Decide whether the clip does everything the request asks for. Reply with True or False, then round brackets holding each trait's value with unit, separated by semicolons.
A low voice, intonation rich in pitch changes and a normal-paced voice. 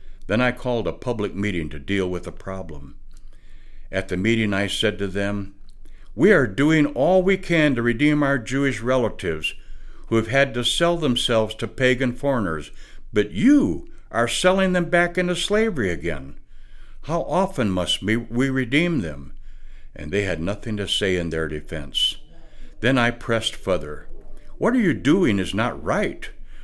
True (115 Hz; 6.3 semitones; 165 wpm)